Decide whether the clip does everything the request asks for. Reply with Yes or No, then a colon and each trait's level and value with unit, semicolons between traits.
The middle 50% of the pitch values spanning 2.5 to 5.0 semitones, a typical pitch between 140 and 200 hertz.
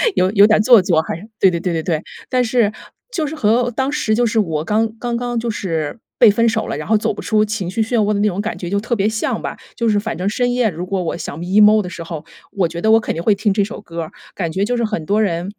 No: average, 3.9 semitones; high, 210 Hz